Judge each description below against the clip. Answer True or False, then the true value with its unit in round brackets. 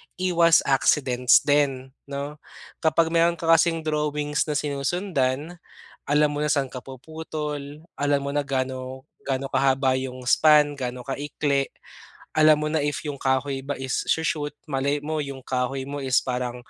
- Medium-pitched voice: True (145 Hz)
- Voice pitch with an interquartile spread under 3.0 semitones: True (2.4 semitones)